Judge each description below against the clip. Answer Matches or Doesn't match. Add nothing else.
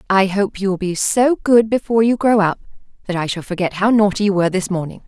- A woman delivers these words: Matches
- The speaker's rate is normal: Doesn't match